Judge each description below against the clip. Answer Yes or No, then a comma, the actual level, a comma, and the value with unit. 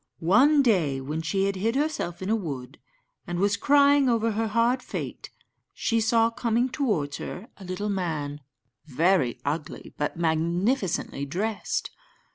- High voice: Yes, high, 195 Hz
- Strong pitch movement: Yes, wide, 6.3 semitones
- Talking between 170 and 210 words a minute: No, average, 145 wpm